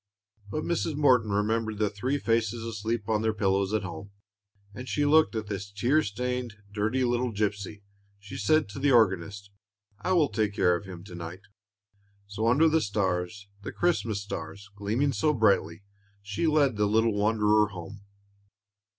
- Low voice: Yes, low, 105 Hz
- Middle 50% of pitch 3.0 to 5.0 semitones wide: Yes, average, 3.7 semitones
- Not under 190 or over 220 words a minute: No, average, 170 wpm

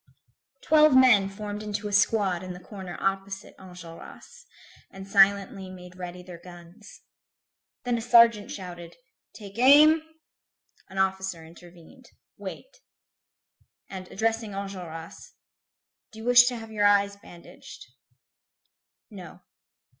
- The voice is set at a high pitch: Yes, high, 200 Hz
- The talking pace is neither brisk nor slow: No, slow, 115 wpm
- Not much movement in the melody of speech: No, average, 3.6 semitones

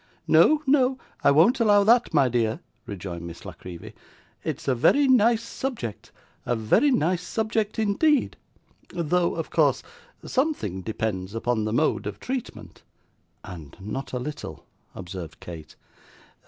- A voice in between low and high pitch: Yes, medium, 150 Hz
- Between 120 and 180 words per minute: Yes, average, 140 wpm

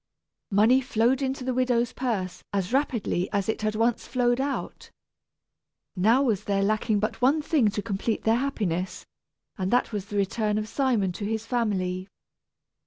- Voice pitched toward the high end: Yes, high, 220 Hz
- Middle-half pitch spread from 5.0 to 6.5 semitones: No, average, 3.8 semitones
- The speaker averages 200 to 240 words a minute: No, average, 165 wpm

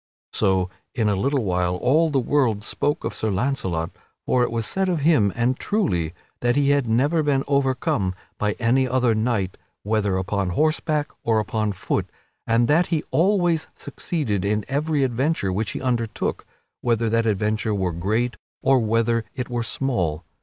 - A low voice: Yes, low, 115 Hz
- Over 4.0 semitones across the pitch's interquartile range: Yes, average, 5.2 semitones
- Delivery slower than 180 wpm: Yes, average, 165 wpm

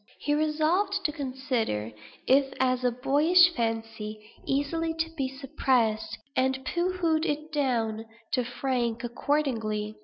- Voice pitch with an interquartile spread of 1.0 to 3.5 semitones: No, average, 4.7 semitones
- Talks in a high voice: Yes, very high, 265 Hz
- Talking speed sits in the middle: No, slow, 125 wpm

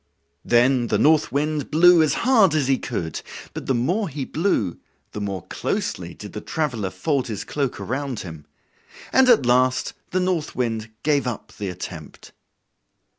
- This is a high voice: No, low, 135 Hz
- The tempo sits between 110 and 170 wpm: Yes, average, 165 wpm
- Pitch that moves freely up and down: Yes, wide, 5.7 semitones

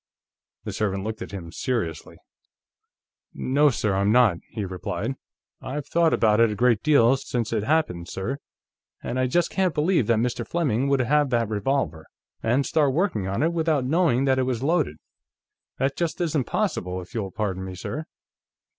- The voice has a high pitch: No, low, 125 Hz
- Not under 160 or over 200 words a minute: Yes, average, 175 wpm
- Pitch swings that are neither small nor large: No, wide, 6.0 semitones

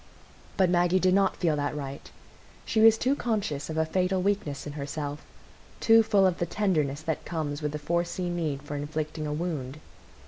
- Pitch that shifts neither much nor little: Yes, average, 4.2 semitones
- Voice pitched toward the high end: No, medium, 160 Hz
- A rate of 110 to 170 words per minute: No, average, 180 wpm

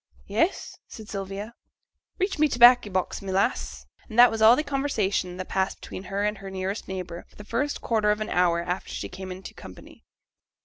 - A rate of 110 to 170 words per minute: No, fast, 205 wpm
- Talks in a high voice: Yes, high, 200 Hz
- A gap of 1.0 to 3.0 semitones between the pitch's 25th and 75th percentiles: No, average, 3.7 semitones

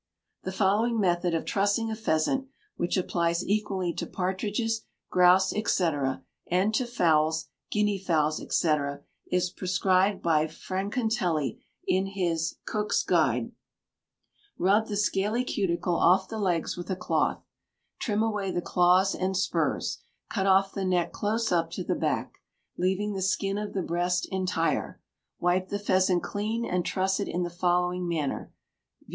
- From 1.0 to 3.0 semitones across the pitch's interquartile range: Yes, average, 2.7 semitones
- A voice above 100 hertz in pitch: Yes, medium, 185 Hz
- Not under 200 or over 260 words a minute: No, average, 145 wpm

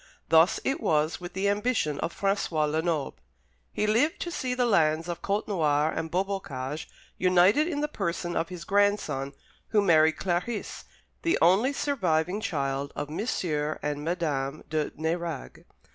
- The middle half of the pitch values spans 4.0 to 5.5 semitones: Yes, average, 4.7 semitones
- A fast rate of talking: No, average, 145 wpm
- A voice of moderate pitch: Yes, medium, 175 Hz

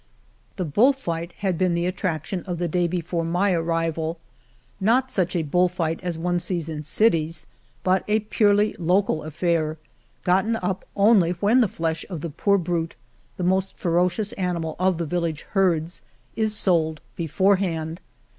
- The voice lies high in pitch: No, medium, 175 Hz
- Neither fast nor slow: Yes, average, 165 wpm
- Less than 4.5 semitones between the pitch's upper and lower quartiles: Yes, average, 2.7 semitones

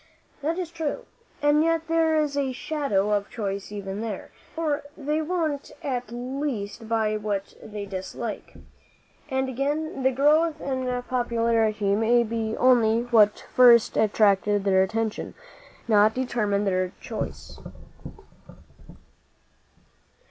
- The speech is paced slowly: Yes, slow, 120 wpm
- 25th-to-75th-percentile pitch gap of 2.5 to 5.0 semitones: No, wide, 5.4 semitones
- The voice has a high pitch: Yes, high, 235 Hz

